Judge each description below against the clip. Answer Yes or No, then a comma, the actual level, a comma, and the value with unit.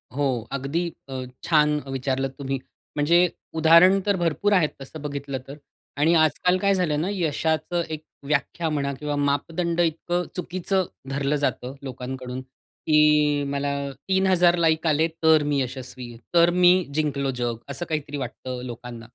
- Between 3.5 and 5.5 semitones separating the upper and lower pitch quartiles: Yes, average, 3.8 semitones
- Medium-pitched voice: Yes, medium, 150 Hz